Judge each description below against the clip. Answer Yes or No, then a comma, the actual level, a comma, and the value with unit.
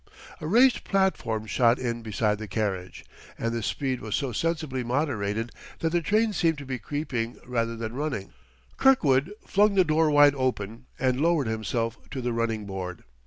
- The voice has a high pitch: No, low, 125 Hz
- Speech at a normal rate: Yes, average, 170 wpm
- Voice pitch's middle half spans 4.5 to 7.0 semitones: Yes, wide, 5.4 semitones